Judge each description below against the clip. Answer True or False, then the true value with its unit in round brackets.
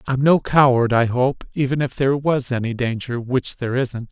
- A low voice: True (130 Hz)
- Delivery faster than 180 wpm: True (205 wpm)